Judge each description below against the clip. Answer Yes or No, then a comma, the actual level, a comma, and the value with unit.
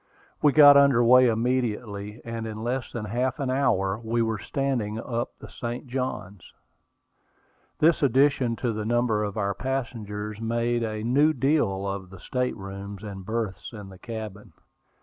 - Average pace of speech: Yes, average, 160 wpm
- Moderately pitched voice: No, low, 115 Hz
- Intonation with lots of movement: No, average, 3.4 semitones